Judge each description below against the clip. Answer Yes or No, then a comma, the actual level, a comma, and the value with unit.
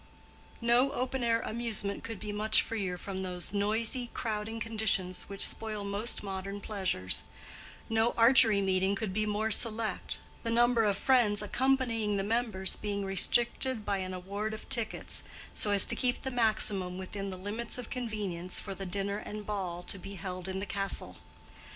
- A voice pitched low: No, high, 210 Hz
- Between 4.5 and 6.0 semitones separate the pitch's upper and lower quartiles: No, average, 2.8 semitones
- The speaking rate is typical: Yes, average, 170 wpm